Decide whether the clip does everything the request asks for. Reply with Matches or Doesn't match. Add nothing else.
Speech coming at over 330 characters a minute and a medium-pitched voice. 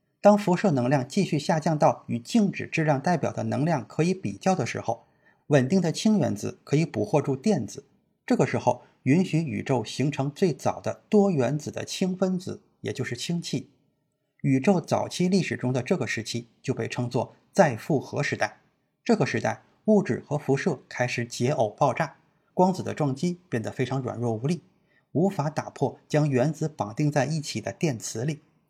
Doesn't match